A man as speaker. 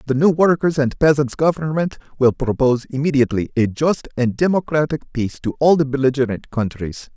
Yes: male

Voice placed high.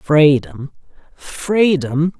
No: medium, 155 Hz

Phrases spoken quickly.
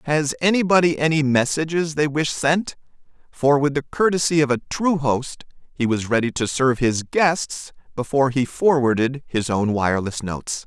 No: average, 165 wpm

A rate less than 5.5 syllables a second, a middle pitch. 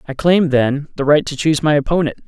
No: 5.9 syllables/s; medium, 150 Hz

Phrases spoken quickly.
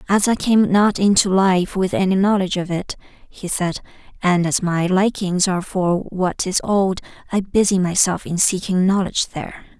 No: average, 180 wpm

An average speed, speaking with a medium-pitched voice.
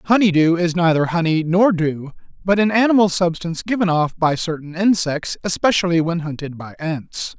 Yes: average, 160 wpm; medium, 170 Hz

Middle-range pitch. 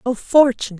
No: high, 240 Hz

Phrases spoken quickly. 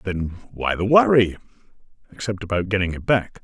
No: average, 155 wpm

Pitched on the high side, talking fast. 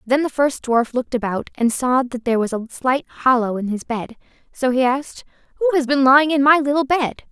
Yes: very high, 255 Hz; fast, 230 wpm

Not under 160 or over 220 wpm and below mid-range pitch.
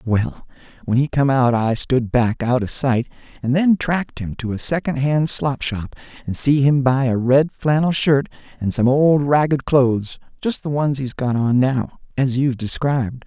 Yes: average, 190 wpm; low, 130 Hz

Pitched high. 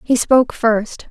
Yes: high, 230 Hz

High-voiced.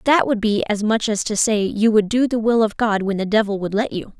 Yes: high, 215 Hz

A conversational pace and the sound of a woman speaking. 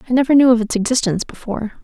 No: fast, 230 wpm; female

